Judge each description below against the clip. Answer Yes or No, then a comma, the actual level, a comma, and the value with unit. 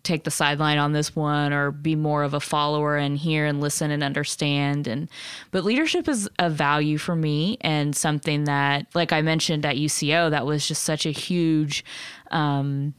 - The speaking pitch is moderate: Yes, medium, 150 Hz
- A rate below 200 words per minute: Yes, average, 190 wpm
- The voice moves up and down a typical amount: No, narrow, 1.6 semitones